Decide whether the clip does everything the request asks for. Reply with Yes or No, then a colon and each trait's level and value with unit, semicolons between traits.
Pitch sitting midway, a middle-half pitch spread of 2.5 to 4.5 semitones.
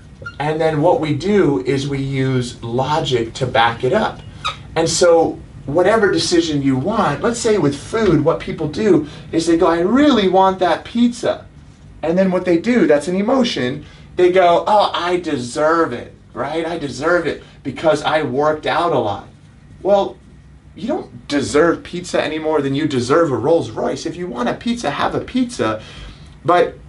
No: medium, 155 Hz; average, 4.9 semitones